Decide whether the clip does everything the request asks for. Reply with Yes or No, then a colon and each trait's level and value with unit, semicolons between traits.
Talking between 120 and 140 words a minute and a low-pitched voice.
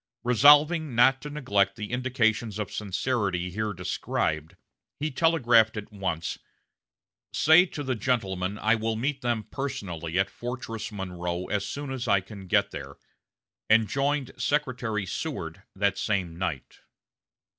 Yes: slow, 135 wpm; low, 110 Hz